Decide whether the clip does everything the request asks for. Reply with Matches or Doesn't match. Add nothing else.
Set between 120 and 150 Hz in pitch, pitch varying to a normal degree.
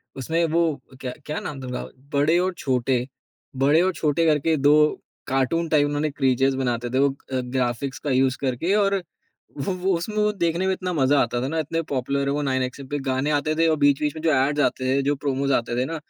Matches